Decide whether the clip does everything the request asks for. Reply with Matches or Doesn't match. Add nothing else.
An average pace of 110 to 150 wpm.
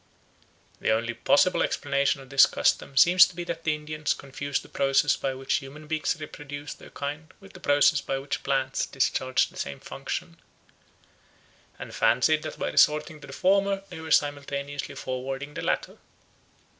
Doesn't match